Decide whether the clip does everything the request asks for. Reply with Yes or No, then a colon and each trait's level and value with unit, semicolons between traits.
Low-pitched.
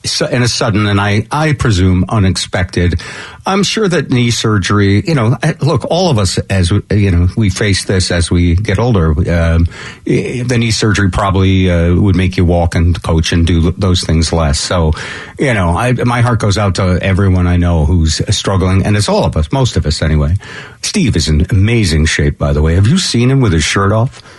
Yes: very low, 95 Hz